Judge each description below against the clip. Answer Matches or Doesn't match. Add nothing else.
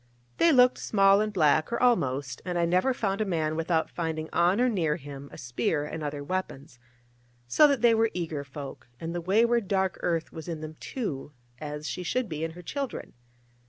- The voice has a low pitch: Doesn't match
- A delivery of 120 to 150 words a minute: Doesn't match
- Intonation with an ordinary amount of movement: Doesn't match